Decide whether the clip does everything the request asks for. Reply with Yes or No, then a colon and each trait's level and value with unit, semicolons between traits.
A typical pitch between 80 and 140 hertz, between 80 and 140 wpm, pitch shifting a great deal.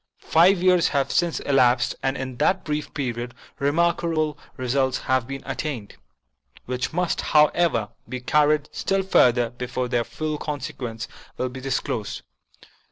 No: low, 135 Hz; slow, 135 wpm; average, 3.7 semitones